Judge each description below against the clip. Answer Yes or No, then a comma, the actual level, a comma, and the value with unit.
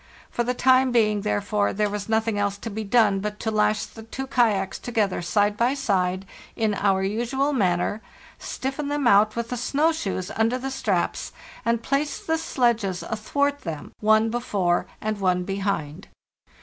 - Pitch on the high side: Yes, high, 215 Hz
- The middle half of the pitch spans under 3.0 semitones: No, average, 3.7 semitones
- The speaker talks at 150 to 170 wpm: Yes, average, 165 wpm